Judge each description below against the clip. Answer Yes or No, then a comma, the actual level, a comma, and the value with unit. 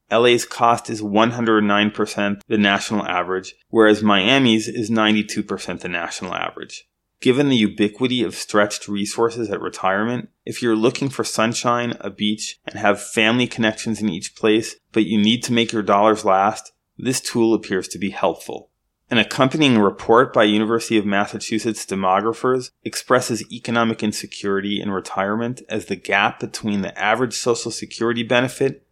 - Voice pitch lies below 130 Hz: Yes, low, 110 Hz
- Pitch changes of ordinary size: No, narrow, 2.3 semitones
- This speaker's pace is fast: No, average, 150 wpm